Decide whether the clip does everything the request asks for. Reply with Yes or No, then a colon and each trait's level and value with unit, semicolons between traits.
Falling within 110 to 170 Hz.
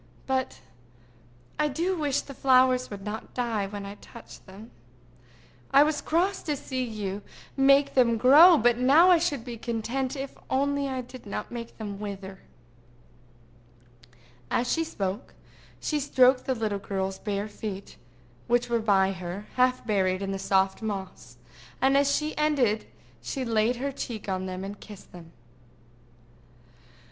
No: high, 235 Hz